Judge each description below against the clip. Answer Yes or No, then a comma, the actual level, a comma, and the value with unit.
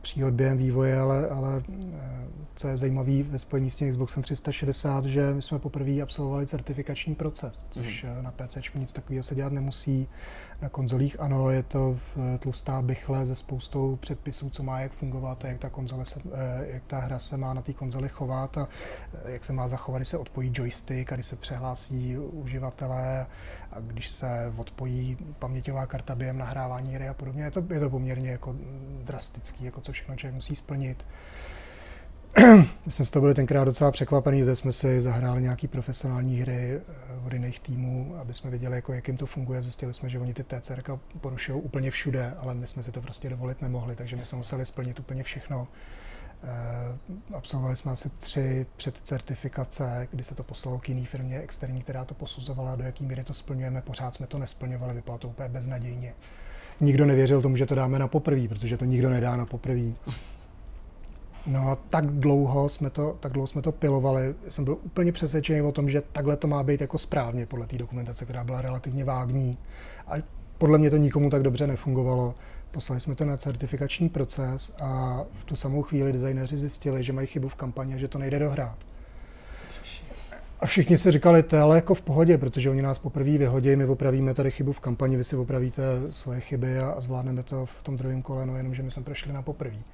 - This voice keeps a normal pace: No, fast, 195 wpm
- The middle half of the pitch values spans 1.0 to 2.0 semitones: Yes, narrow, 1.7 semitones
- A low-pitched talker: Yes, low, 130 Hz